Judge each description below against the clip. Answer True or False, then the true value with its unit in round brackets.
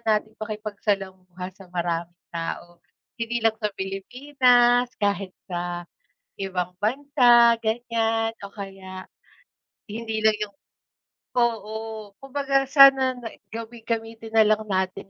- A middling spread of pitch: True (3.6 semitones)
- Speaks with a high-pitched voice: True (220 Hz)